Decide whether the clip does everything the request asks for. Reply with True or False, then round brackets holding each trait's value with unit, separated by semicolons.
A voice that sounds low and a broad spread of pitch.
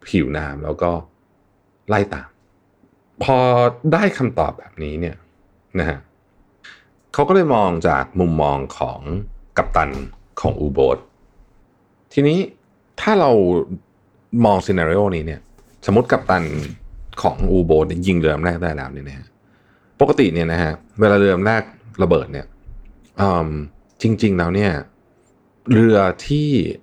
False (95 Hz; 4.3 semitones)